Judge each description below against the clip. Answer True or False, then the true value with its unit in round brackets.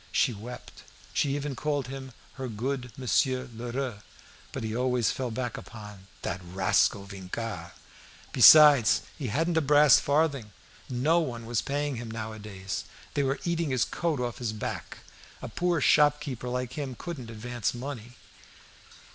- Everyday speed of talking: True (155 wpm)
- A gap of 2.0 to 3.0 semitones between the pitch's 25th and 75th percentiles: False (4.2 semitones)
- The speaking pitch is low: True (125 Hz)